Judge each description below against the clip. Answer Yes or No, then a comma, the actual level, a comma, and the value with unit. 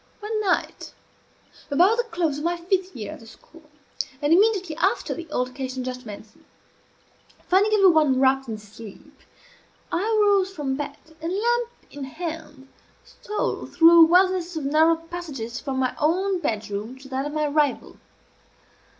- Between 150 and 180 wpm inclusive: Yes, average, 155 wpm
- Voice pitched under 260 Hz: No, very high, 315 Hz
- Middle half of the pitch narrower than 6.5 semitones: Yes, wide, 5.6 semitones